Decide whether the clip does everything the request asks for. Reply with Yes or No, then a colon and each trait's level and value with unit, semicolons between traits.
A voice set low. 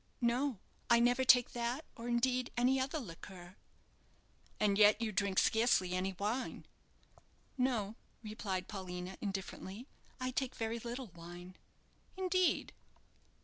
No: high, 230 Hz